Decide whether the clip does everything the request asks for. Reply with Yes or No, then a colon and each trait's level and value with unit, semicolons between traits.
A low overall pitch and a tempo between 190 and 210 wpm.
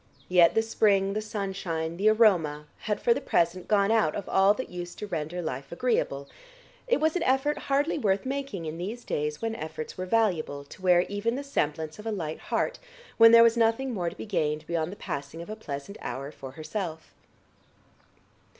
No: high, 195 Hz; average, 195 wpm